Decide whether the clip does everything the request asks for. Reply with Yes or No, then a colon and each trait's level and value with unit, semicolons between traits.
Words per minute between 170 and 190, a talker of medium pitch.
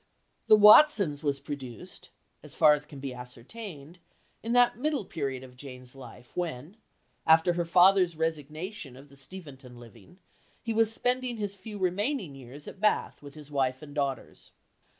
No: average, 160 wpm; medium, 155 Hz